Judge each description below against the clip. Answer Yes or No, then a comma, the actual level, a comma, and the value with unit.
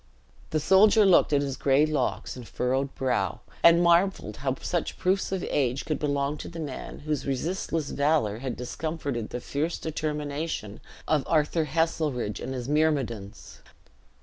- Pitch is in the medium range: Yes, medium, 145 Hz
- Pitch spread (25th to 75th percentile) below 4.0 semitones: Yes, average, 3.6 semitones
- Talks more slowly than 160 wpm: Yes, average, 150 wpm